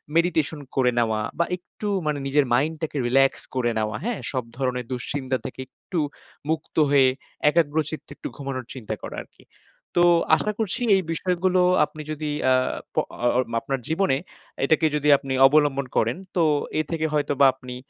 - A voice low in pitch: No, medium, 145 Hz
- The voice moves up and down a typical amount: Yes, average, 3.6 semitones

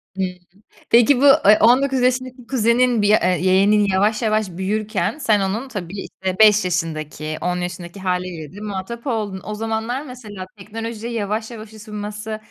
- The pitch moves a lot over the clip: No, average, 3.4 semitones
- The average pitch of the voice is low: No, high, 210 Hz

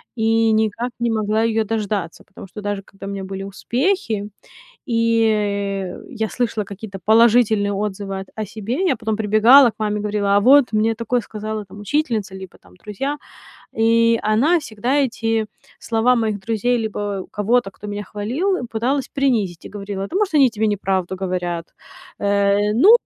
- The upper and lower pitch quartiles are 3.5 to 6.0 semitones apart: No, narrow, 2.4 semitones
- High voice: Yes, high, 215 Hz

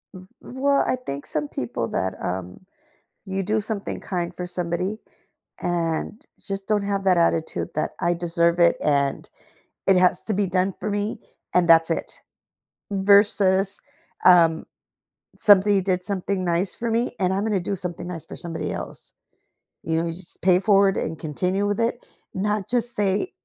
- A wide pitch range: No, average, 3.0 semitones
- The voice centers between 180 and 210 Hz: Yes, medium, 185 Hz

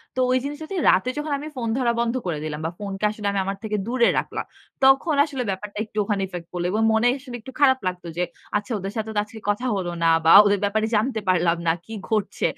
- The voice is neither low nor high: No, high, 215 Hz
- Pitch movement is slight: No, average, 5.0 semitones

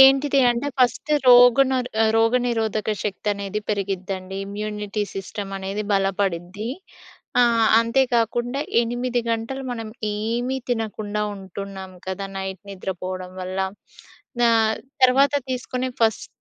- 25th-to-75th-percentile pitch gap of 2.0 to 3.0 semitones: No, average, 3.8 semitones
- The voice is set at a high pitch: Yes, high, 220 Hz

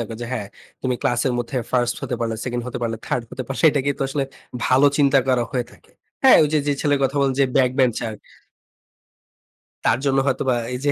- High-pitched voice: No, low, 130 Hz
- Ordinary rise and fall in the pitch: No, narrow, 2.3 semitones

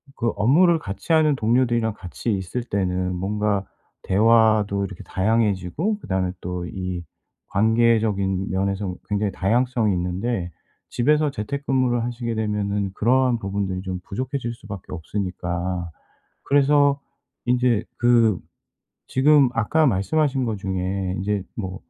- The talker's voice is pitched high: No, low, 105 Hz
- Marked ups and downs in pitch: No, average, 4.3 semitones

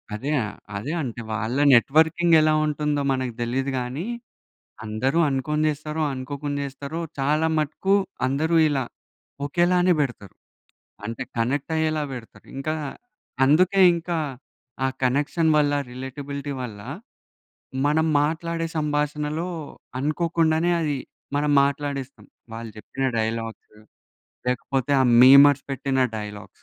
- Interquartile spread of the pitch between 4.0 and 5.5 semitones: No, average, 3.2 semitones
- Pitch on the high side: No, medium, 145 Hz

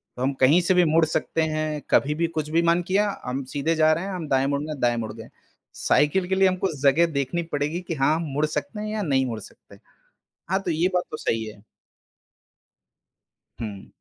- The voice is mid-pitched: Yes, medium, 155 Hz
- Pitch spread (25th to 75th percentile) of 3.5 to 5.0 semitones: Yes, average, 4.0 semitones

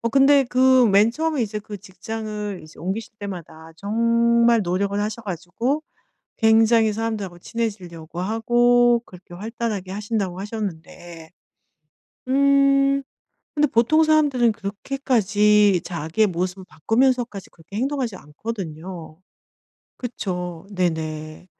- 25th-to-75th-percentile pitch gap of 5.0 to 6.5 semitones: No, average, 4.6 semitones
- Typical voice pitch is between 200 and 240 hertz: Yes, high, 210 Hz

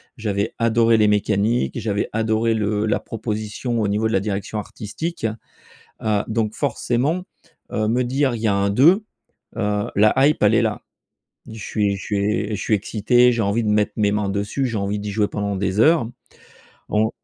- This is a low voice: Yes, low, 110 Hz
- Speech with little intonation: Yes, narrow, 2.0 semitones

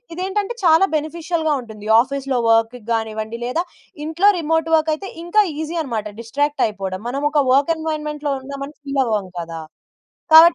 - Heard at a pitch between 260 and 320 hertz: Yes, very high, 290 Hz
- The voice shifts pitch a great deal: Yes, wide, 6.0 semitones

